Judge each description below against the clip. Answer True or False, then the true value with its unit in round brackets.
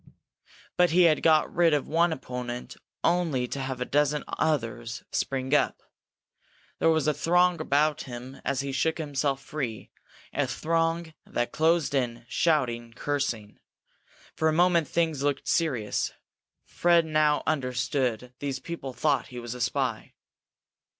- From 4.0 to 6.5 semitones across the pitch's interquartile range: True (4.3 semitones)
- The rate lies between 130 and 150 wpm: True (145 wpm)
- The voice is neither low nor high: True (145 Hz)